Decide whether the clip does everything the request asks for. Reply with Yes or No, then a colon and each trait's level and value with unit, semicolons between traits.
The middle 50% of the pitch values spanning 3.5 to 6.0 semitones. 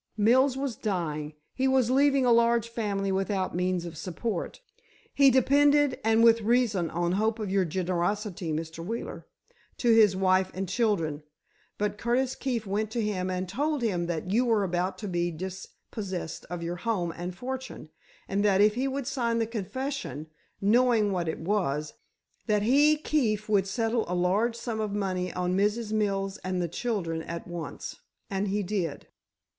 Yes: average, 4.5 semitones